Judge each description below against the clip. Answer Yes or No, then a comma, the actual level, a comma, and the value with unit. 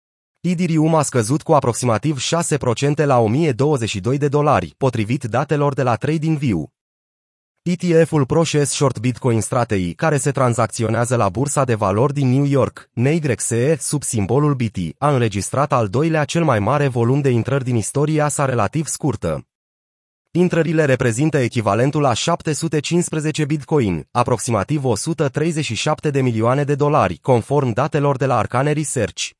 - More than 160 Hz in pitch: No, medium, 140 Hz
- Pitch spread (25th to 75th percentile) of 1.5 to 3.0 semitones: No, average, 4.1 semitones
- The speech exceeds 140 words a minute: No, average, 135 wpm